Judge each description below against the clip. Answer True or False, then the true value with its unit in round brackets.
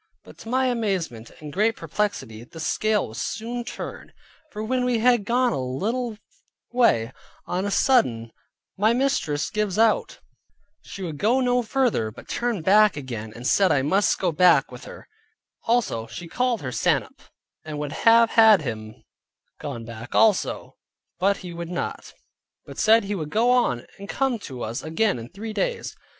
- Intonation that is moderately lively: False (8.2 semitones)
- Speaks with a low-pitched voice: False (200 Hz)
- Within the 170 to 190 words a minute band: True (175 wpm)